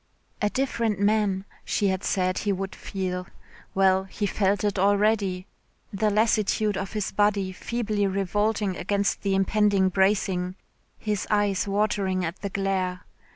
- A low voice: No, high, 200 Hz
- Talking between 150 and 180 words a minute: No, average, 140 wpm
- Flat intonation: Yes, narrow, 1.7 semitones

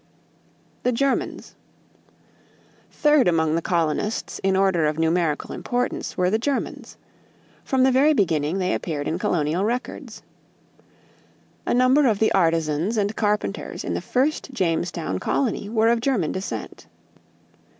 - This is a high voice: Yes, high, 195 Hz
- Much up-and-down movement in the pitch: Yes, wide, 7.0 semitones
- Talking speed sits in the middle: No, slow, 130 wpm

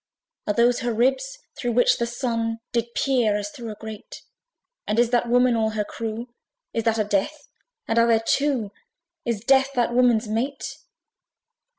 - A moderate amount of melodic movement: No, narrow, 2.0 semitones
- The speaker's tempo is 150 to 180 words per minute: Yes, average, 175 wpm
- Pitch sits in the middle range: No, high, 235 Hz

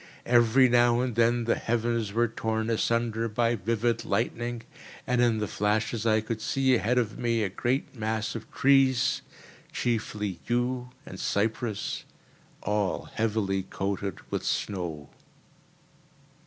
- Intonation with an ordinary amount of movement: No, narrow, 2.2 semitones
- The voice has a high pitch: No, low, 115 Hz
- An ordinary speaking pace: No, slow, 130 wpm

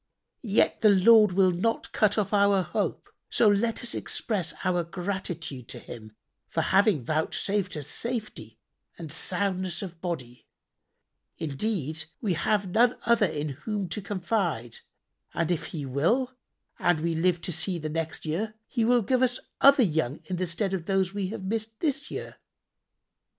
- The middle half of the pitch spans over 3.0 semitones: Yes, average, 4.9 semitones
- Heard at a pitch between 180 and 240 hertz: Yes, medium, 185 Hz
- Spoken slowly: No, average, 160 wpm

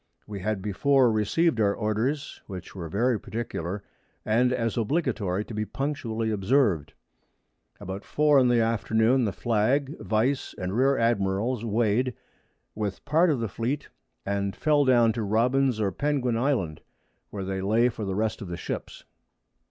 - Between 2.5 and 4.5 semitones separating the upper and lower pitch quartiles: Yes, average, 4.2 semitones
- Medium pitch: No, low, 115 Hz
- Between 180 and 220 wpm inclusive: No, average, 155 wpm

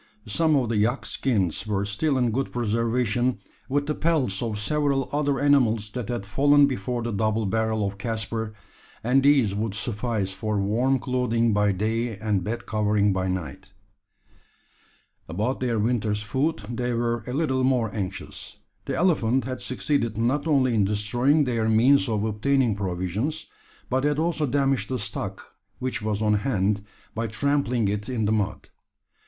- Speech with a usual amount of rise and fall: Yes, average, 4.0 semitones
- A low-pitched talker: Yes, low, 115 Hz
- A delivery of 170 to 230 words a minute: No, average, 160 wpm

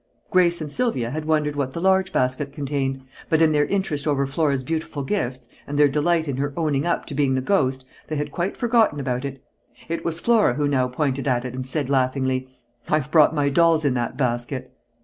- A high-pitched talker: No, medium, 145 Hz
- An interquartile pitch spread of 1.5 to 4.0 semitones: Yes, average, 3.5 semitones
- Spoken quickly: Yes, fast, 210 wpm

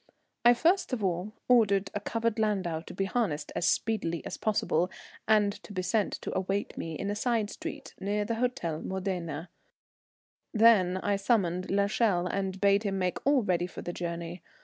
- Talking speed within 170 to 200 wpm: Yes, average, 175 wpm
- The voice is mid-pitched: No, high, 200 Hz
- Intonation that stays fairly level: No, average, 3.5 semitones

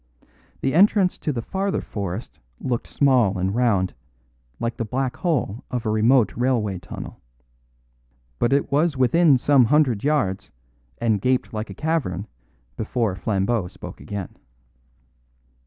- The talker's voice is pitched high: No, low, 120 Hz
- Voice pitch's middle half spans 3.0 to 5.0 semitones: No, wide, 5.4 semitones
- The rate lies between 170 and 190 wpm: No, slow, 135 wpm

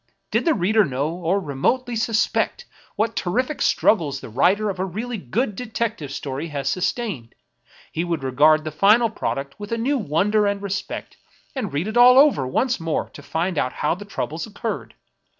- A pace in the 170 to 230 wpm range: Yes, average, 180 wpm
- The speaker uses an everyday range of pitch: No, wide, 6.7 semitones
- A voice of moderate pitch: No, high, 195 Hz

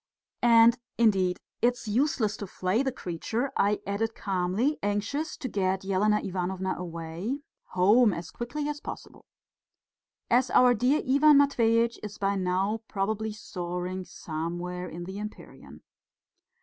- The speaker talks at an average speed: No, slow, 130 wpm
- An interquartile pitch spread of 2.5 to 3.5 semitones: No, average, 4.5 semitones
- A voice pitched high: Yes, high, 210 Hz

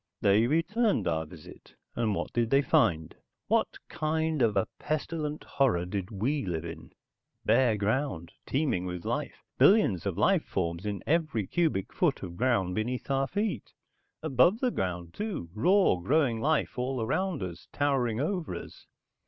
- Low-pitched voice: Yes, low, 125 Hz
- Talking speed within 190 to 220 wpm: No, average, 155 wpm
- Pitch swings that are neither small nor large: No, wide, 8.6 semitones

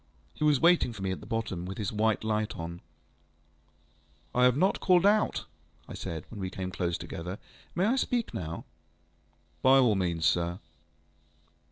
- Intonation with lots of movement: Yes, wide, 7.1 semitones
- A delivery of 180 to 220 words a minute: No, average, 170 wpm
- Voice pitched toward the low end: Yes, low, 105 Hz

